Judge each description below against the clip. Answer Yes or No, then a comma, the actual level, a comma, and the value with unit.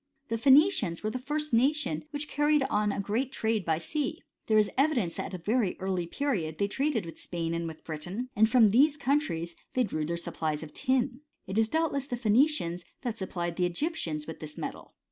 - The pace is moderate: No, fast, 215 wpm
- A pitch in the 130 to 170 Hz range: No, high, 220 Hz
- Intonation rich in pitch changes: Yes, wide, 8.3 semitones